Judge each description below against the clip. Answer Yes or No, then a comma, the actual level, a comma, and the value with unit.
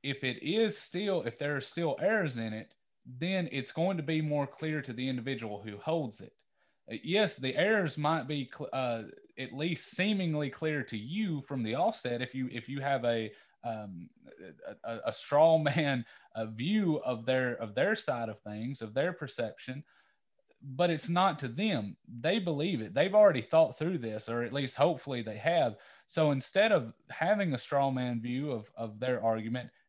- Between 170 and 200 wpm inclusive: Yes, average, 190 wpm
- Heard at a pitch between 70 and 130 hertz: No, medium, 140 Hz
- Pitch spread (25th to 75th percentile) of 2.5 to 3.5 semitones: No, average, 5.2 semitones